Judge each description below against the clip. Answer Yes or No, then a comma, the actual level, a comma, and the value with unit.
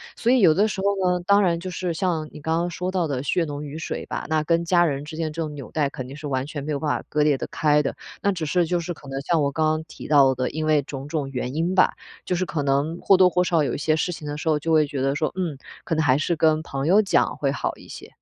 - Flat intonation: No, average, 3.2 semitones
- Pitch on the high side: No, medium, 155 Hz